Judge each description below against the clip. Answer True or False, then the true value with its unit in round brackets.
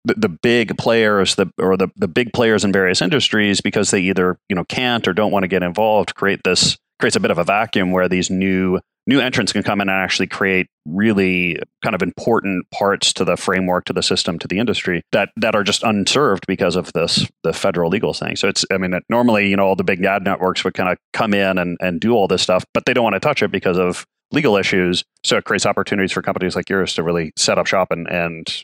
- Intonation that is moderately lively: False (2.1 semitones)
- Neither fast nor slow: False (250 wpm)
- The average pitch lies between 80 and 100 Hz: True (95 Hz)